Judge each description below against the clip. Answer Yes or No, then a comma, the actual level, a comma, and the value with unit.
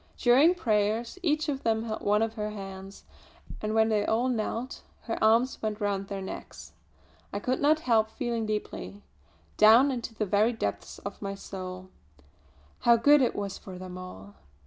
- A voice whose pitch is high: Yes, high, 220 Hz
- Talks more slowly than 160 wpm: No, average, 170 wpm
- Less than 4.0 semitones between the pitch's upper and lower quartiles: Yes, average, 3.1 semitones